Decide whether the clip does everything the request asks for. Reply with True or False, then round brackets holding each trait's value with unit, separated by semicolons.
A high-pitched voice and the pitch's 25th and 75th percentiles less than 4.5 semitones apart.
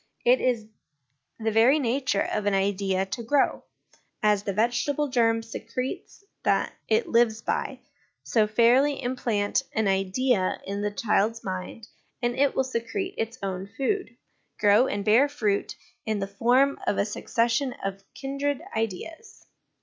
True (230 Hz; 4.1 semitones)